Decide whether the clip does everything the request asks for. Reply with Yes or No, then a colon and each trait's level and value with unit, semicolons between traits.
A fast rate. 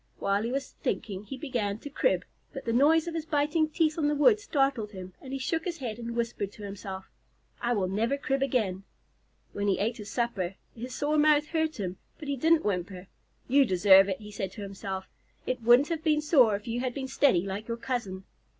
Yes: fast, 220 wpm